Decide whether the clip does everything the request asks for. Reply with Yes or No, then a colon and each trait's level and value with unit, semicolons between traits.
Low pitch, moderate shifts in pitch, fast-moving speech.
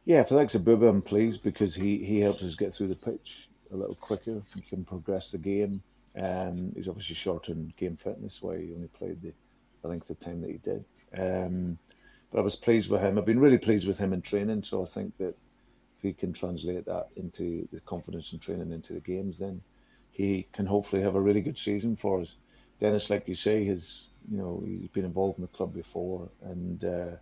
No: very low, 95 Hz; narrow, 2.3 semitones; fast, 230 wpm